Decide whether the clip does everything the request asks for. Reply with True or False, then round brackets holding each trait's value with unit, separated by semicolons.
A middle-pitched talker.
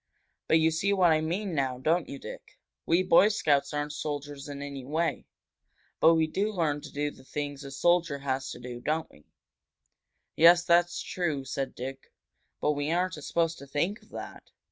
True (150 Hz)